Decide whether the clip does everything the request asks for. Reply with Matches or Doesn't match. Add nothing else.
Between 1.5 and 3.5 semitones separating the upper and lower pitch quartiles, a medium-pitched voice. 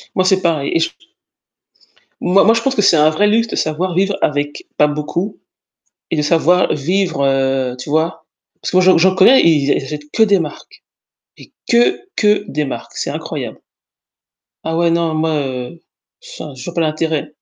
Doesn't match